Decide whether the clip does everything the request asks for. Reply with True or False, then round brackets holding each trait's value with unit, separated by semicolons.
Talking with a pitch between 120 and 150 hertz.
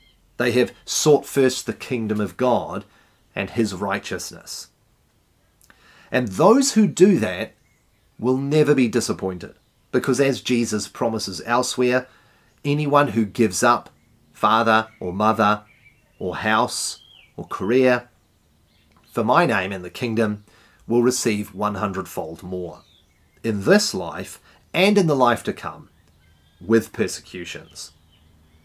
False (110 Hz)